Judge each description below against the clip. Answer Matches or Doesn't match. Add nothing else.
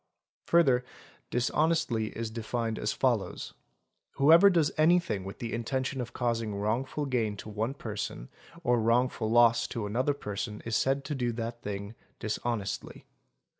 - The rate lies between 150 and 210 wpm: Doesn't match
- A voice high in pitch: Doesn't match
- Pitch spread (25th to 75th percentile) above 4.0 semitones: Doesn't match